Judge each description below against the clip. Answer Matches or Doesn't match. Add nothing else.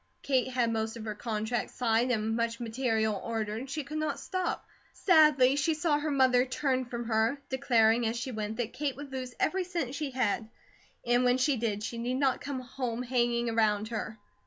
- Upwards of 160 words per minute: Matches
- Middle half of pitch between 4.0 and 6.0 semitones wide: Doesn't match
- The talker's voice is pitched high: Matches